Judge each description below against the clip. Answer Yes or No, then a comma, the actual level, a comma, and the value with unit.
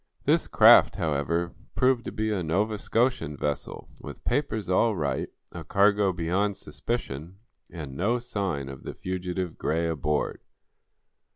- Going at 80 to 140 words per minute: Yes, slow, 135 wpm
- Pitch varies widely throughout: No, average, 4.9 semitones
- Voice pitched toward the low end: Yes, very low, 90 Hz